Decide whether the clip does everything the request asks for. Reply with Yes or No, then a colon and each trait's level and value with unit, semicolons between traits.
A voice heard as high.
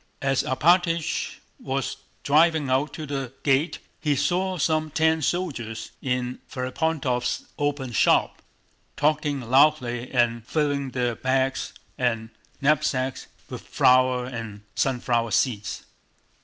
No: low, 135 Hz